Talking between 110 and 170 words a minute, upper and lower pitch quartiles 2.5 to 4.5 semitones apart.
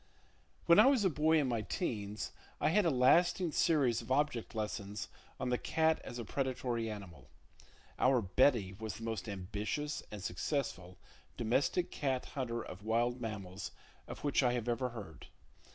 No: average, 165 wpm; average, 5.2 semitones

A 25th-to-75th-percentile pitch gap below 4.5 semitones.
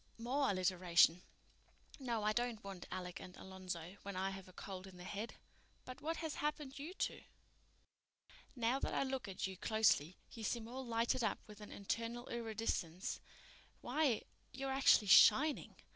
No: average, 5.3 semitones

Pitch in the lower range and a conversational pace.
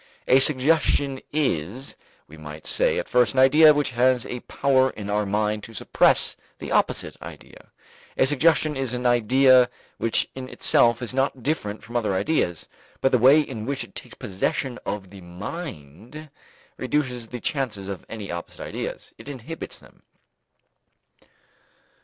Yes: low, 125 Hz; average, 155 wpm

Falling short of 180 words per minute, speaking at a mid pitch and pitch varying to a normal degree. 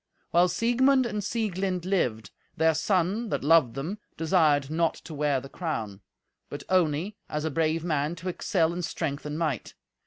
Yes: average, 165 wpm; medium, 165 Hz; average, 3.9 semitones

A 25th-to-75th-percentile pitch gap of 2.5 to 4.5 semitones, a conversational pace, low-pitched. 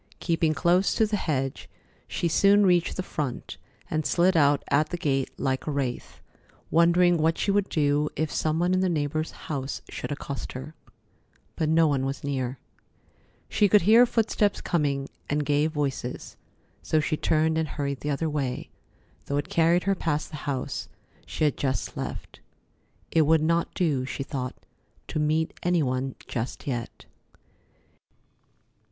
No: average, 3.4 semitones; average, 160 wpm; medium, 155 Hz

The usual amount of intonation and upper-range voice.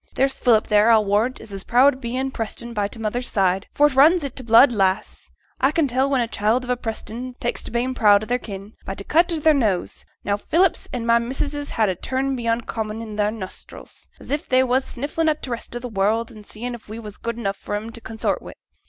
Yes: average, 3.5 semitones; high, 235 Hz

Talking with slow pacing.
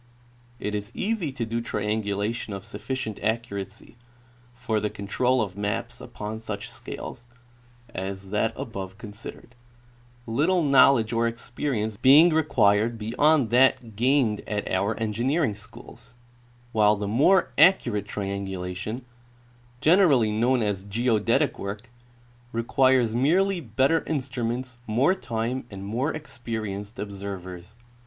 Yes: slow, 115 wpm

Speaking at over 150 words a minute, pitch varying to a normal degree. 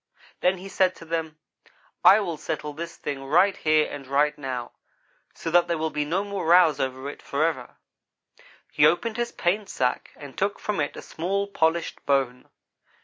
Yes: average, 180 wpm; average, 4.2 semitones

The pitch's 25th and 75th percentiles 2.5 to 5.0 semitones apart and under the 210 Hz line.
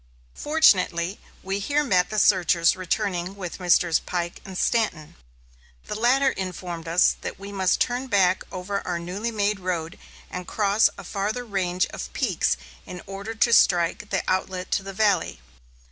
Yes: average, 2.8 semitones; high, 190 Hz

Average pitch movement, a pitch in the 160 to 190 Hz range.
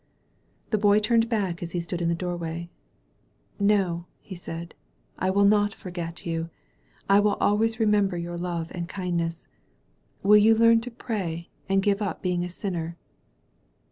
Yes: average, 3.4 semitones; medium, 185 Hz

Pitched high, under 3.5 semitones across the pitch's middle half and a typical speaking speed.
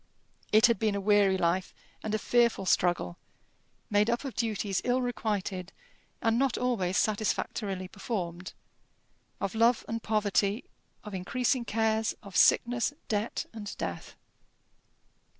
No: high, 215 Hz; average, 3.1 semitones; slow, 130 wpm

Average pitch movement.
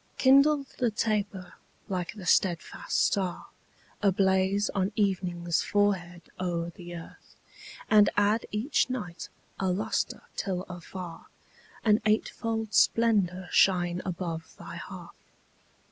Yes: average, 3.1 semitones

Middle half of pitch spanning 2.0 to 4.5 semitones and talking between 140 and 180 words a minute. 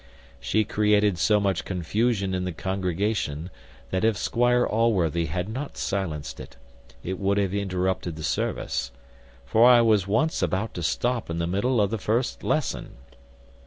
Yes: average, 3.5 semitones; average, 160 wpm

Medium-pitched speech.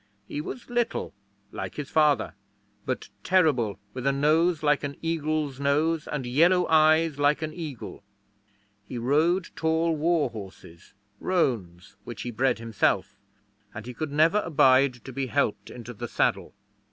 Yes: medium, 145 Hz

